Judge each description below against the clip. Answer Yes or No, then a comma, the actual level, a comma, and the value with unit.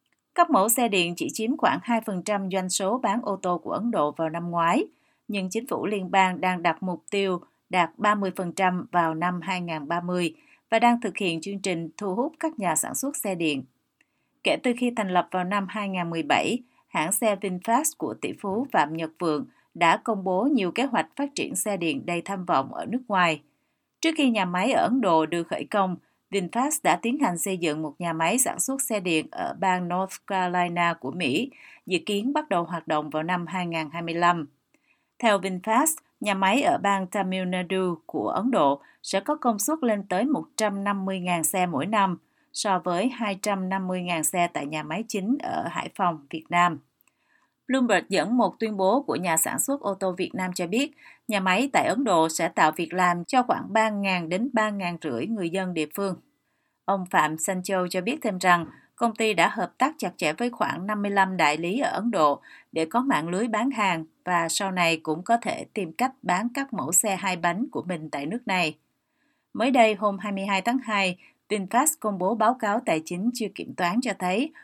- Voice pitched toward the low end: No, high, 195 Hz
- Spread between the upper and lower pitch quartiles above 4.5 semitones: Yes, average, 5.0 semitones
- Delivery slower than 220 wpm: Yes, average, 200 wpm